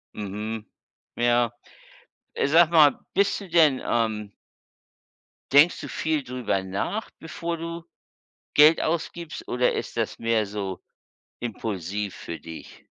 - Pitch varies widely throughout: Yes, wide, 7.5 semitones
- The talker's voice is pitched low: Yes, low, 120 Hz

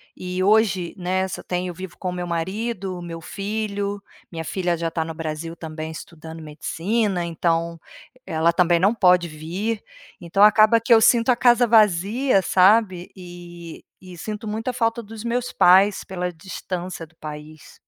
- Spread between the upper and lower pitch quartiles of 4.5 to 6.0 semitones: No, average, 4.0 semitones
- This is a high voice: No, medium, 180 Hz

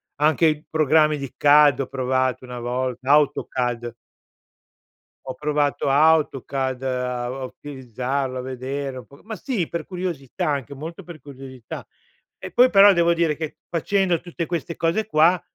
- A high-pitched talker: No, medium, 145 Hz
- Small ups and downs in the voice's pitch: No, average, 4.1 semitones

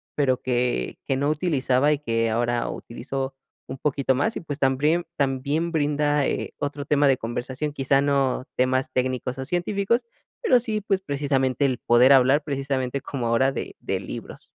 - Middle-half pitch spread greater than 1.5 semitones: Yes, narrow, 2.4 semitones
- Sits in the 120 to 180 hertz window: Yes, low, 135 Hz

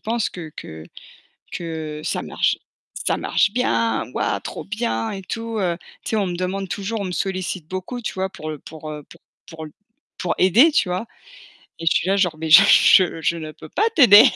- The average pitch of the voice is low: No, medium, 185 Hz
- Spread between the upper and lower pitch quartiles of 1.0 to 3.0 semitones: No, average, 4.2 semitones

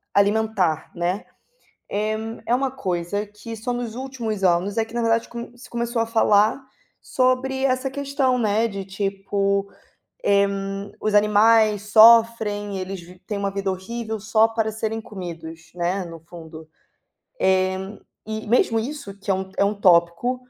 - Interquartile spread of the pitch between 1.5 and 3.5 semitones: Yes, average, 3.1 semitones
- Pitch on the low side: No, high, 210 Hz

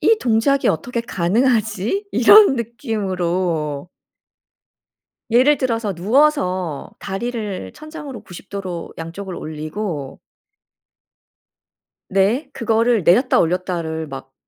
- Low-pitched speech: No, high, 205 Hz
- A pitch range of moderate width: No, wide, 5.8 semitones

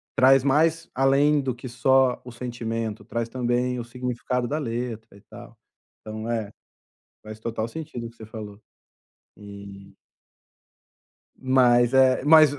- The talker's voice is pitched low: Yes, low, 120 Hz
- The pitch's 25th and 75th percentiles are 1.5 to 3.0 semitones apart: Yes, average, 2.7 semitones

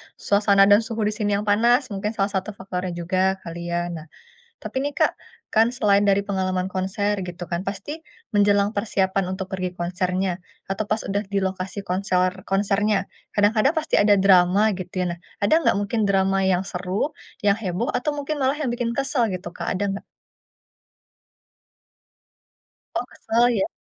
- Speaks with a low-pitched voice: No, high, 200 Hz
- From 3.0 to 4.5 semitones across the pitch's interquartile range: No, narrow, 2.4 semitones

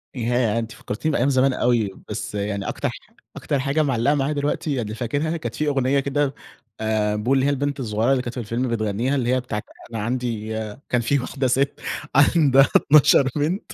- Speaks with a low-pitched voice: Yes, low, 130 Hz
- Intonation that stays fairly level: No, average, 3.6 semitones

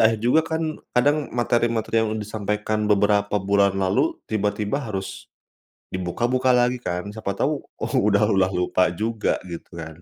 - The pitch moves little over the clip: No, average, 3.2 semitones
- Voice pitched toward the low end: Yes, low, 105 Hz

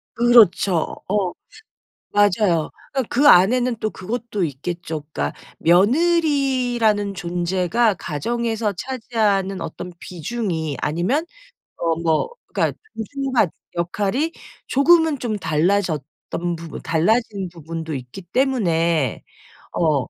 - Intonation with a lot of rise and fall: Yes, wide, 6.1 semitones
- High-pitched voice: Yes, high, 195 Hz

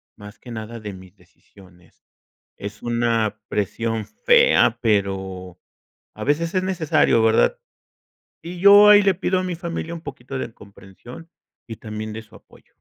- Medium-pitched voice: No, low, 115 Hz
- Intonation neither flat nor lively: No, wide, 8.3 semitones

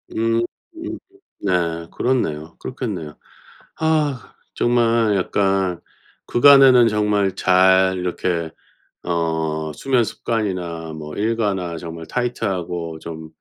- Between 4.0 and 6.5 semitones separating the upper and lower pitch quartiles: Yes, wide, 5.5 semitones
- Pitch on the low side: Yes, very low, 95 Hz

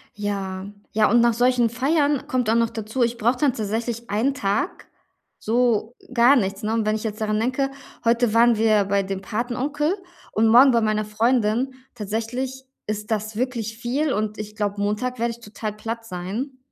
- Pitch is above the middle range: Yes, high, 230 Hz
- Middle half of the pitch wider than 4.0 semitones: No, average, 2.7 semitones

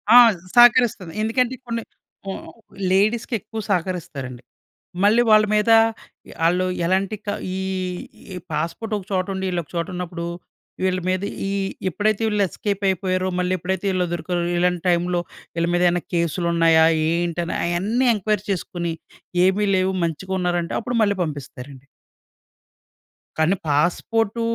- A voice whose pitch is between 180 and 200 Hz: Yes, medium, 185 Hz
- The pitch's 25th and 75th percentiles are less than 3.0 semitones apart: No, average, 3.3 semitones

